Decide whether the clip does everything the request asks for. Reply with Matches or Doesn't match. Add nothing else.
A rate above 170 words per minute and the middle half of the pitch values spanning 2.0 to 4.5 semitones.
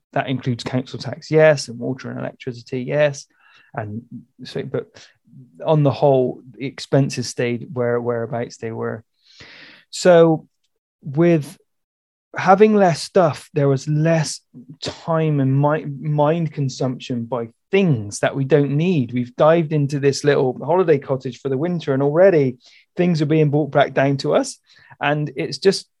Doesn't match